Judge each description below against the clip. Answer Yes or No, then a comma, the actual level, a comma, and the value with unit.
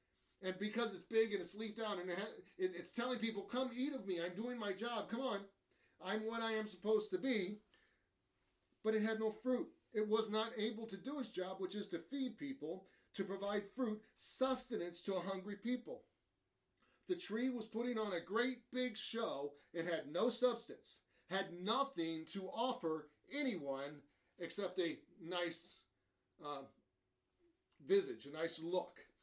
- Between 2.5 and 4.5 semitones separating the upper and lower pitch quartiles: No, average, 5.1 semitones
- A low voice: No, high, 210 Hz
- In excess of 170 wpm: No, average, 165 wpm